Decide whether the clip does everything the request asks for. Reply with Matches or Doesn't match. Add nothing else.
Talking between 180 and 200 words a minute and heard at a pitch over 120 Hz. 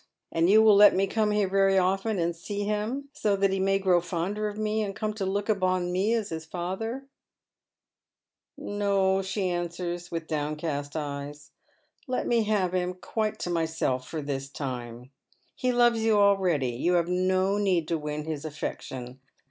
Matches